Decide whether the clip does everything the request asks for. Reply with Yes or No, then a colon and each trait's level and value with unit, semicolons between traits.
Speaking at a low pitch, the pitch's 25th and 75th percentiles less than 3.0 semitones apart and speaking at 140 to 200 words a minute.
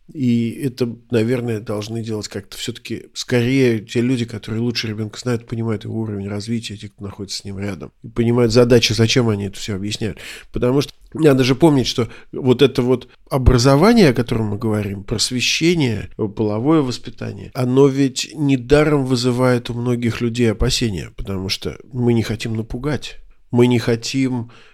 Yes: low, 120 Hz; narrow, 2.6 semitones; fast, 160 wpm